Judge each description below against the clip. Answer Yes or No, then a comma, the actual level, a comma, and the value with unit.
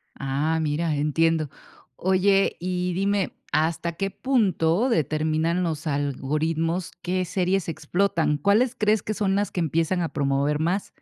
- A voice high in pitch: No, medium, 170 Hz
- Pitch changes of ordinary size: Yes, average, 3.6 semitones